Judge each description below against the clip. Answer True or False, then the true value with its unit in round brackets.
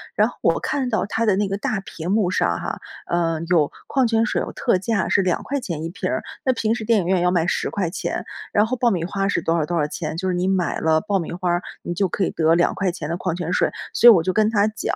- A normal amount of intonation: True (4.0 semitones)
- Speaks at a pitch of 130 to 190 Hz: True (185 Hz)